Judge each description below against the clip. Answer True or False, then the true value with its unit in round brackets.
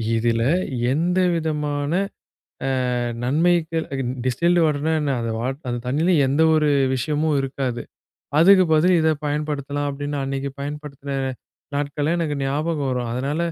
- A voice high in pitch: False (145 Hz)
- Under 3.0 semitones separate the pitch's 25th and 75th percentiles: True (2.4 semitones)